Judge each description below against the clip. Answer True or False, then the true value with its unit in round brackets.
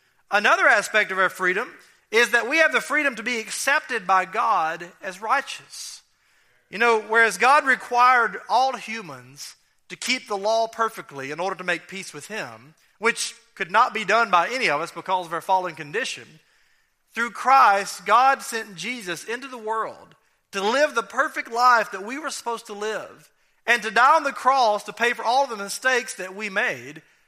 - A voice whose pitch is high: True (225 Hz)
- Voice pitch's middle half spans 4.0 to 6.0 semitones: True (4.4 semitones)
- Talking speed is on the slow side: False (185 wpm)